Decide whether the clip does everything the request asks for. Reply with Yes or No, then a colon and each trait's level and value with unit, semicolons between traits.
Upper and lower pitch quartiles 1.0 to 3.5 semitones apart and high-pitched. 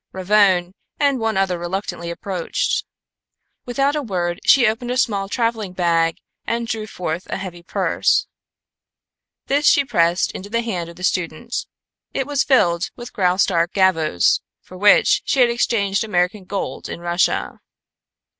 No: average, 4.9 semitones; high, 195 Hz